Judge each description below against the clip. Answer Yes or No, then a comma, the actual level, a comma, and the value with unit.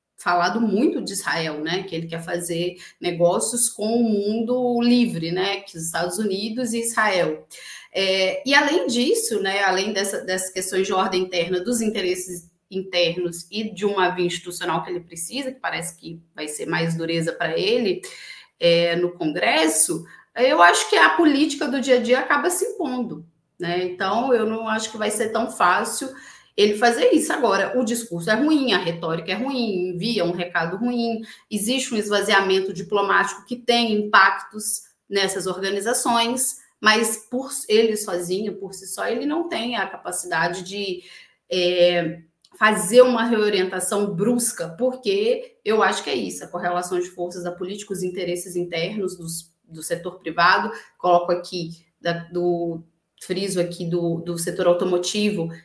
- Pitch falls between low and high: No, high, 195 Hz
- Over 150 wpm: Yes, average, 160 wpm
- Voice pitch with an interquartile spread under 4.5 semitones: No, average, 4.8 semitones